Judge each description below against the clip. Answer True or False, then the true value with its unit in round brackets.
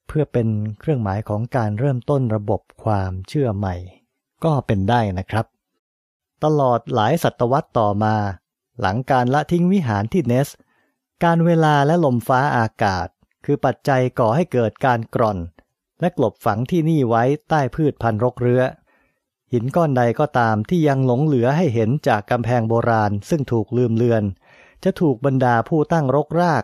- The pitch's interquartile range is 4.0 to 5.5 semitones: True (4.7 semitones)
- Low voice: True (125 Hz)